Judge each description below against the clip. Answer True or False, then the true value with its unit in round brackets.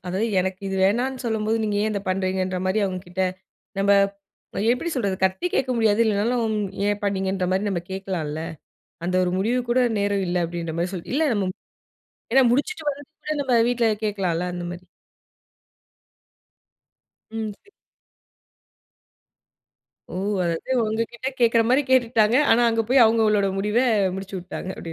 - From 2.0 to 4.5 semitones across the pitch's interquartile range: True (3.9 semitones)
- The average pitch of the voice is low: False (210 Hz)